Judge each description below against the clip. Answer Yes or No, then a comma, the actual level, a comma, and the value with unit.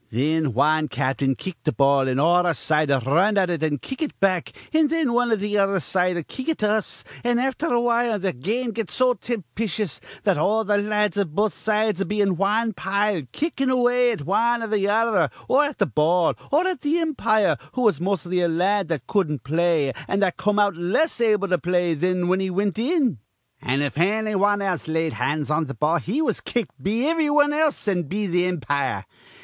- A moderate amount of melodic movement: No, wide, 5.8 semitones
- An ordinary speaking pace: No, fast, 220 wpm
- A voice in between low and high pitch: No, high, 200 Hz